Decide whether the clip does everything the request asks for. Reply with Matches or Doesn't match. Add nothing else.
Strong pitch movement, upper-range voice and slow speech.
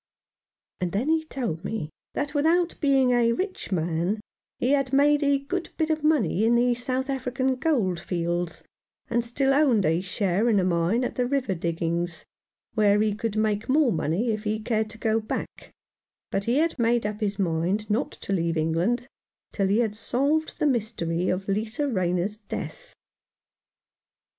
Doesn't match